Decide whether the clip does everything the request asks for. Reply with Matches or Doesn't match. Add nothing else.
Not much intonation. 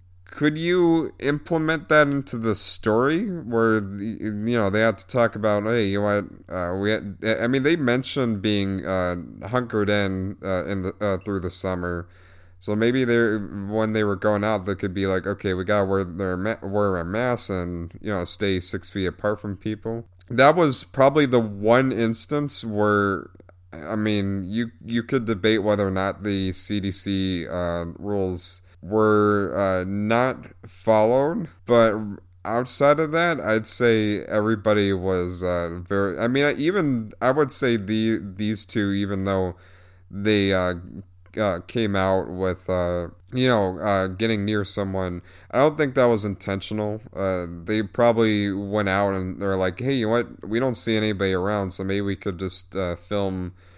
Doesn't match